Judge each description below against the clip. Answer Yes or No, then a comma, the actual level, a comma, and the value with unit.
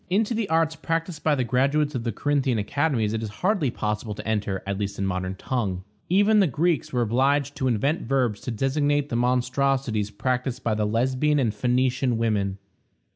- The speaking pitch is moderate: No, low, 125 Hz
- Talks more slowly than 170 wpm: No, average, 190 wpm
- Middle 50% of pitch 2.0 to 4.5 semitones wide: No, average, 5.1 semitones